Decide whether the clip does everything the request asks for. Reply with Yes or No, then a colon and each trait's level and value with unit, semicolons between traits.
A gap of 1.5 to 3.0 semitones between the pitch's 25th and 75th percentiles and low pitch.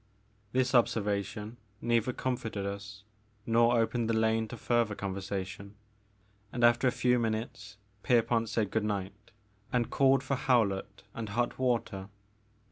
Yes: average, 2.7 semitones; low, 115 Hz